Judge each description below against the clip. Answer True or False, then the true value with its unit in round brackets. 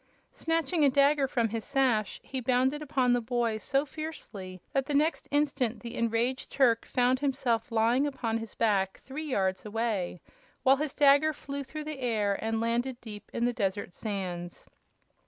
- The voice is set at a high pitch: True (245 Hz)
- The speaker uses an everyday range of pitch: True (3.9 semitones)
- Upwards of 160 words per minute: True (170 wpm)